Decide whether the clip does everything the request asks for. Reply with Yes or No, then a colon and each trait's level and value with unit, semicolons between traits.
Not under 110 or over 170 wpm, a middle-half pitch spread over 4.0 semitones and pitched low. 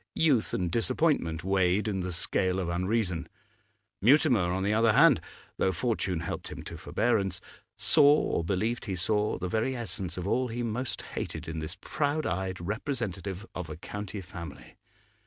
Yes: average, 165 wpm; average, 4.6 semitones; low, 100 Hz